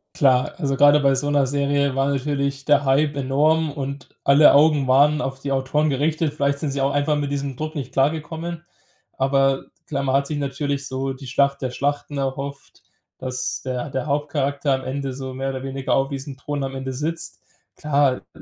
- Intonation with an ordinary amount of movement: No, narrow, 1.4 semitones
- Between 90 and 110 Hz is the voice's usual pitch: No, medium, 140 Hz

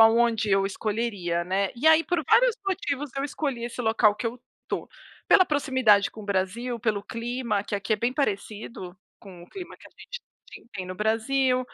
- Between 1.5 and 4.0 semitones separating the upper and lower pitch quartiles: No, average, 4.5 semitones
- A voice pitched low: No, high, 230 Hz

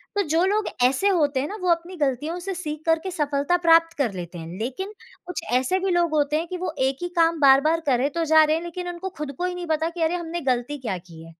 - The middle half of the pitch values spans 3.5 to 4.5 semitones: Yes, average, 4.1 semitones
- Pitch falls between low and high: No, very high, 325 Hz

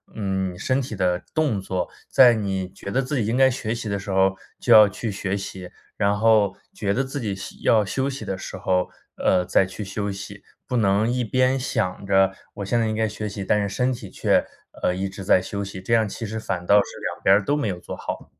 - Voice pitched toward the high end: No, low, 100 Hz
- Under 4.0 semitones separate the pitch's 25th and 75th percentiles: Yes, average, 3.1 semitones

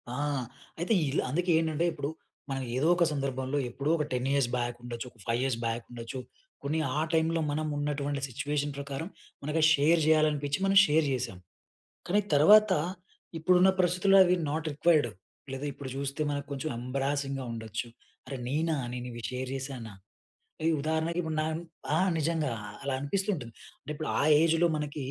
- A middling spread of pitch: Yes, average, 3.3 semitones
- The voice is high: No, medium, 145 Hz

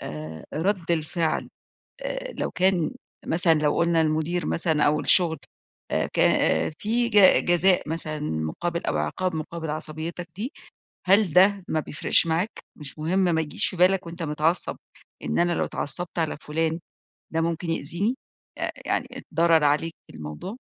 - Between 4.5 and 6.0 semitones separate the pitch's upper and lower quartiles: No, average, 2.7 semitones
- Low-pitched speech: No, medium, 165 Hz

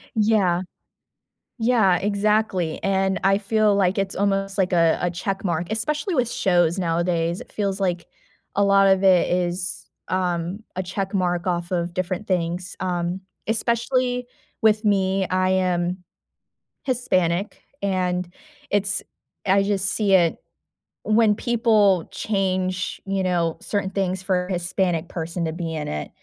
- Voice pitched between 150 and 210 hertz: Yes, high, 190 Hz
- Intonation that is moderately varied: No, narrow, 2.3 semitones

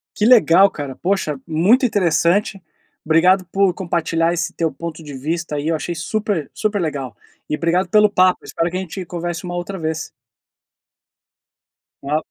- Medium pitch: Yes, medium, 170 Hz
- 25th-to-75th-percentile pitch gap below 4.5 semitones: Yes, average, 3.2 semitones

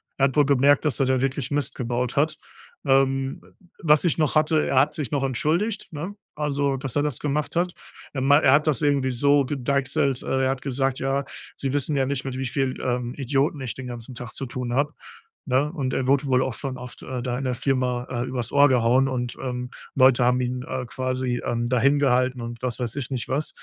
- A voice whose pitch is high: No, low, 135 Hz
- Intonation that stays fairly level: Yes, narrow, 2.2 semitones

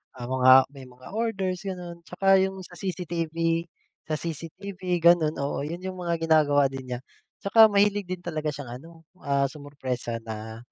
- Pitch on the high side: No, medium, 165 Hz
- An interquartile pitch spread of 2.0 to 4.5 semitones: No, average, 4.9 semitones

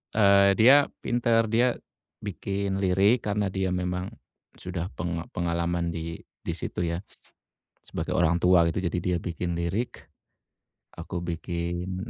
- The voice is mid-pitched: No, very low, 90 Hz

